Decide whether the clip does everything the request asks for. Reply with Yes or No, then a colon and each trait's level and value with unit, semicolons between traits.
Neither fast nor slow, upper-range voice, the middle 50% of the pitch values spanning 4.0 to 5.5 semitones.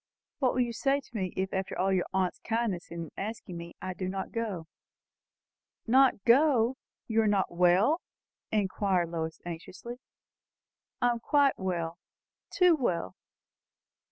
Yes: average, 145 wpm; high, 195 Hz; average, 5.0 semitones